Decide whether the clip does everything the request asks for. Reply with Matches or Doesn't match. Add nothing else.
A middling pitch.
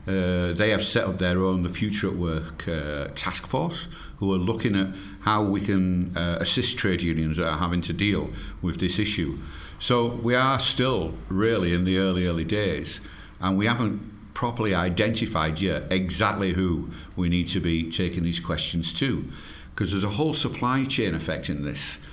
Doesn't match